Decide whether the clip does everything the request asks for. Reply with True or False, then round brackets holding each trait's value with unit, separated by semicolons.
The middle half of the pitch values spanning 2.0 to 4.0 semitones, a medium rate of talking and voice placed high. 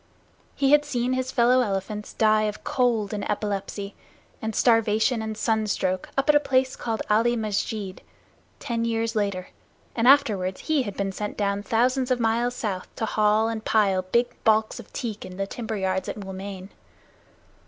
True (3.1 semitones; 165 wpm; 220 Hz)